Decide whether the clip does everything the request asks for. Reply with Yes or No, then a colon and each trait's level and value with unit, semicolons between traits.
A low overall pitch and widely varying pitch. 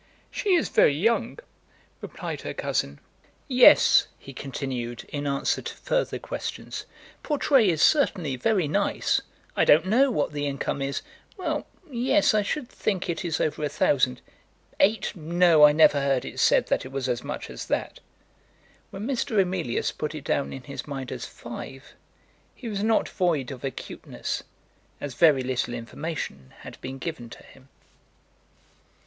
No: medium, 150 Hz; wide, 7.3 semitones